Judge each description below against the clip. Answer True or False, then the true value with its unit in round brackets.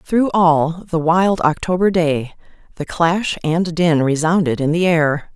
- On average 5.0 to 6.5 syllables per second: False (3.8 syllables/s)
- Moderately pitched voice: True (165 Hz)